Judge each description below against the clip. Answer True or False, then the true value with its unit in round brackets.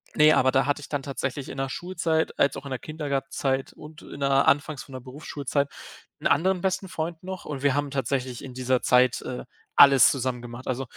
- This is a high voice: False (140 Hz)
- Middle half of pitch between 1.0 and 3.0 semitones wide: True (2.7 semitones)